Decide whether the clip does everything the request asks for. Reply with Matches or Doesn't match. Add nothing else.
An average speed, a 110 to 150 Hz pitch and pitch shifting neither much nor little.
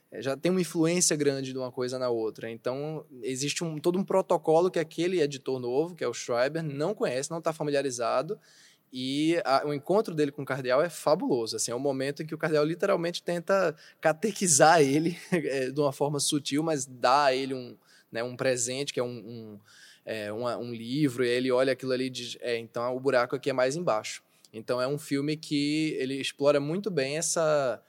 Doesn't match